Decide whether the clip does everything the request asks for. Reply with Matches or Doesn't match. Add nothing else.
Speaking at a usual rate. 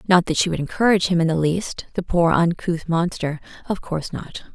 Matches